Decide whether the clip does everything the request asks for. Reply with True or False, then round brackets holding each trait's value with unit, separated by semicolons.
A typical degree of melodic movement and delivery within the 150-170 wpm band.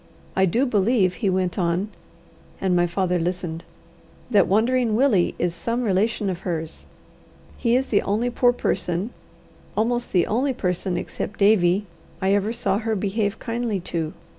True (4.2 semitones; 155 wpm)